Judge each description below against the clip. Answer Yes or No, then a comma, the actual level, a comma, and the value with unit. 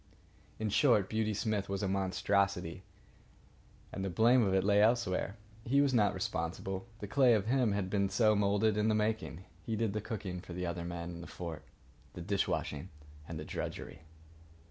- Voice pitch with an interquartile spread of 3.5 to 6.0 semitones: No, average, 3.0 semitones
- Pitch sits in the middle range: No, low, 100 Hz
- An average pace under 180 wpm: No, average, 190 wpm